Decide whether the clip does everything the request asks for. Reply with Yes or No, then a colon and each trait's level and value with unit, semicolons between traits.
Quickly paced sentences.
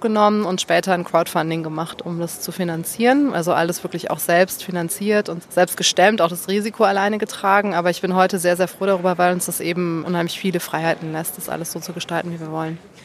Yes: fast, 220 wpm